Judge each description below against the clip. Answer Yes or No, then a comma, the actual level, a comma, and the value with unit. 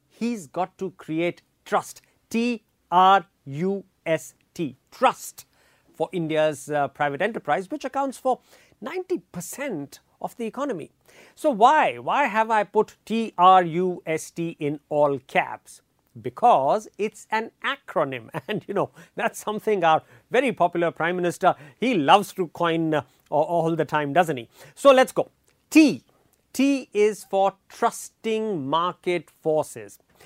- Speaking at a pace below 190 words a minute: Yes, average, 140 wpm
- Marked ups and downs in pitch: Yes, wide, 5.7 semitones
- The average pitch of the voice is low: No, medium, 180 Hz